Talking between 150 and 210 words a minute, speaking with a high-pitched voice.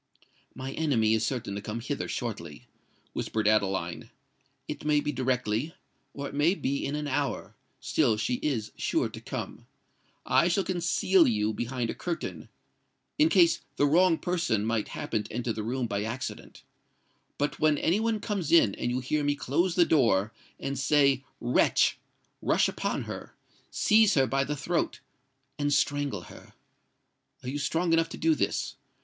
No: average, 155 wpm; medium, 140 Hz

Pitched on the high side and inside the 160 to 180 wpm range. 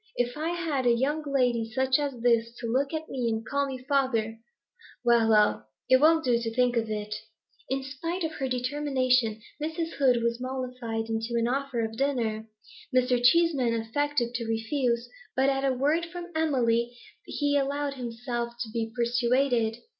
Yes: very high, 250 Hz; average, 170 wpm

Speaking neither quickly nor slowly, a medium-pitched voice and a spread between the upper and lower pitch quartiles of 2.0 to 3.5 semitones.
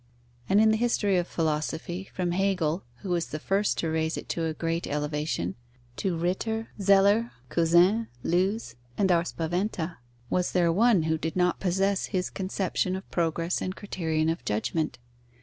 Yes: average, 165 wpm; medium, 175 Hz; average, 3.2 semitones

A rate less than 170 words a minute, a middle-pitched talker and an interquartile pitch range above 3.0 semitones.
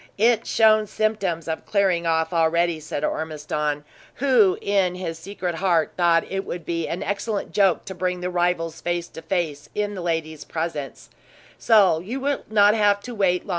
No: average, 175 wpm; medium, 180 Hz; average, 3.7 semitones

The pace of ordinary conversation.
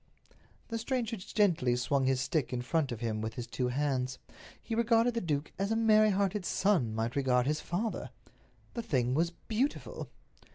Yes: average, 175 wpm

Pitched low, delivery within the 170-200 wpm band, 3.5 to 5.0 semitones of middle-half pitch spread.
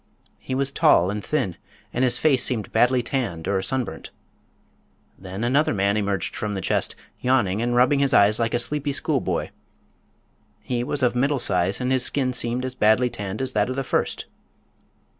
Yes: low, 120 Hz; average, 180 wpm; average, 4.3 semitones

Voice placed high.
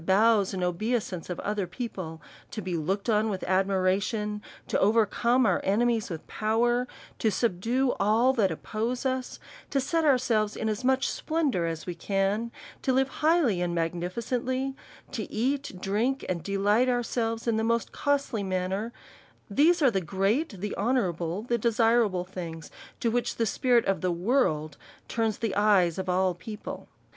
Yes: high, 215 Hz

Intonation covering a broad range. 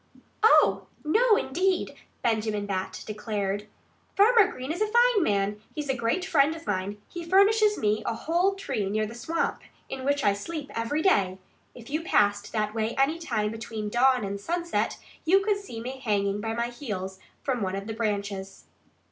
Yes: wide, 8.1 semitones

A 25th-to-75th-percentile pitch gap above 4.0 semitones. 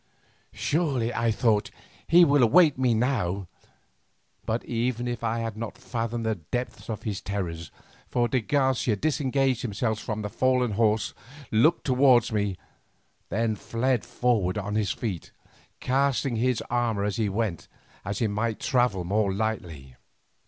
No: average, 3.3 semitones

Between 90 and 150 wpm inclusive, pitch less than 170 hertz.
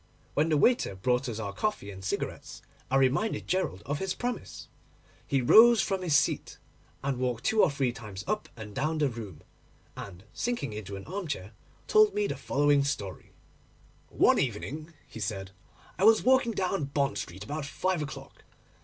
No: average, 170 wpm; medium, 140 Hz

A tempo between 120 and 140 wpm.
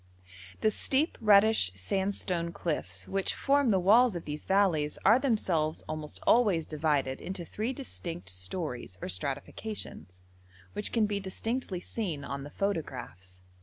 Yes: slow, 135 wpm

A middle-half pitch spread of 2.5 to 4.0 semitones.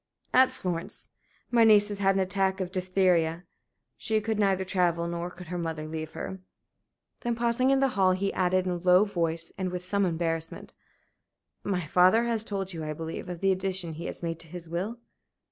Yes: average, 2.9 semitones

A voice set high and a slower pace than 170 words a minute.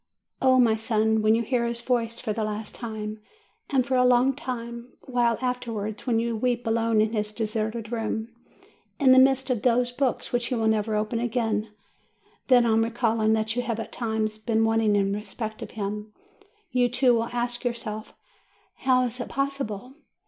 No: high, 230 Hz; average, 180 wpm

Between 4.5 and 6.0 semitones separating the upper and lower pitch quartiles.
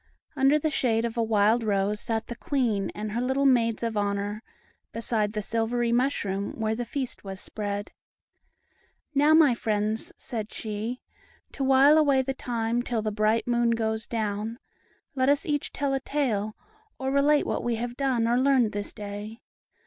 No: average, 3.7 semitones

